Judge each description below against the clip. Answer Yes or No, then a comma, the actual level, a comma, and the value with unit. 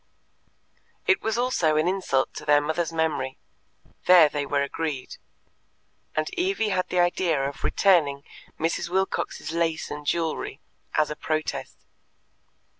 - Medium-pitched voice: Yes, medium, 160 Hz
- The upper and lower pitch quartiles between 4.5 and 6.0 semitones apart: No, average, 3.5 semitones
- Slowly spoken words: Yes, slow, 130 wpm